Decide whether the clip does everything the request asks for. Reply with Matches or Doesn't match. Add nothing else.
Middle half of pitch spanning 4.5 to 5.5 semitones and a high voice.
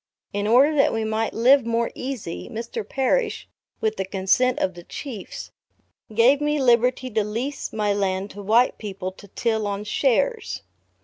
Doesn't match